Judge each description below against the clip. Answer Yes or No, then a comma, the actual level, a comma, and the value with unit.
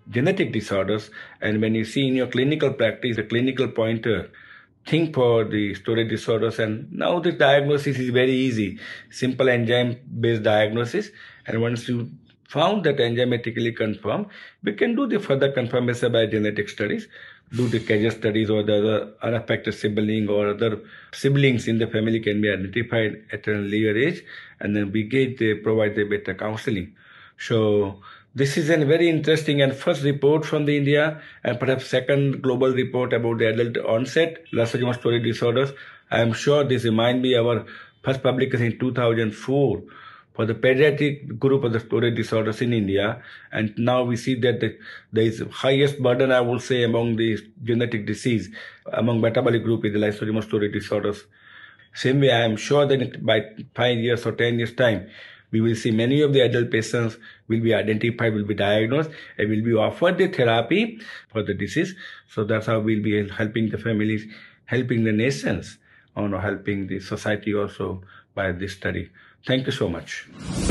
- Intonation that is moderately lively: Yes, average, 3.1 semitones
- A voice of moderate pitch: No, low, 115 Hz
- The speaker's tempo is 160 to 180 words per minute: Yes, average, 175 wpm